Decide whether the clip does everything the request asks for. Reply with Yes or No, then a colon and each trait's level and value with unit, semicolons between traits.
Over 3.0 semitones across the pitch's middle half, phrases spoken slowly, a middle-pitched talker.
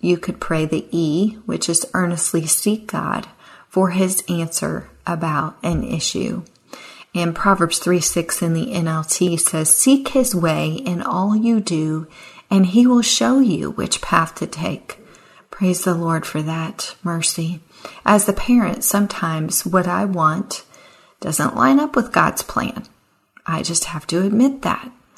No: average, 4.0 semitones; average, 155 wpm; medium, 180 Hz